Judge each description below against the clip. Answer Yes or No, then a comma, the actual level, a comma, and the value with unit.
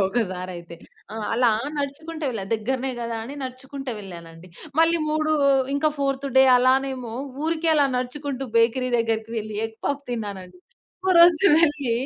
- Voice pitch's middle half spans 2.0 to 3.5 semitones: No, average, 4.4 semitones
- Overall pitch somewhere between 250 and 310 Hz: Yes, very high, 255 Hz